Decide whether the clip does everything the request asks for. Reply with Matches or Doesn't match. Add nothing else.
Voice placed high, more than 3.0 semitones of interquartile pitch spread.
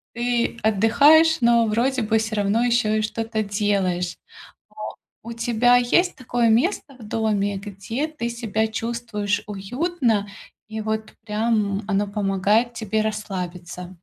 Doesn't match